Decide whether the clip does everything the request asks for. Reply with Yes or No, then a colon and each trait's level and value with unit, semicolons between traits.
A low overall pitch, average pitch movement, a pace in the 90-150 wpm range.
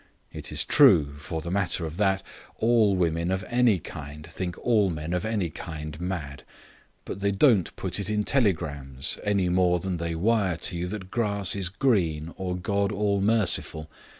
No: very low, 95 Hz; average, 3.6 semitones; average, 175 wpm